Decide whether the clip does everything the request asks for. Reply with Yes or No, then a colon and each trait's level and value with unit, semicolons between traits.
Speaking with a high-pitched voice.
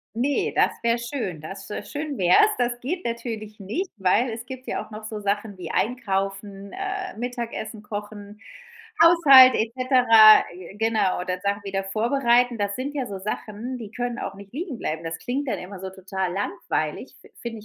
Yes: high, 220 Hz